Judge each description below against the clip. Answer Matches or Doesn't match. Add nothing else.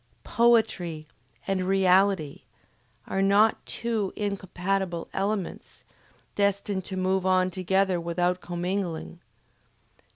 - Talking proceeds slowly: Matches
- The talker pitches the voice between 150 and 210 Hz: Matches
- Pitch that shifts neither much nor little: Doesn't match